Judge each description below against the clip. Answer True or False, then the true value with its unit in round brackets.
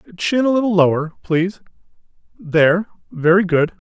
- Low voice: False (175 Hz)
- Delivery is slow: True (110 wpm)